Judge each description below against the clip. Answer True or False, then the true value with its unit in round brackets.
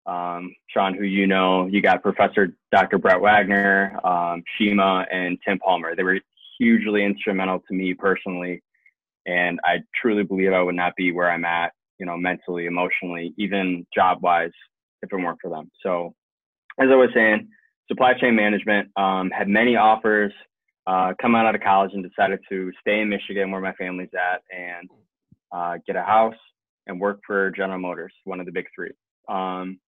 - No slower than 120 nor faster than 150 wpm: False (180 wpm)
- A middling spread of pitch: False (2.1 semitones)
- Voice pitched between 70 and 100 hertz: True (95 Hz)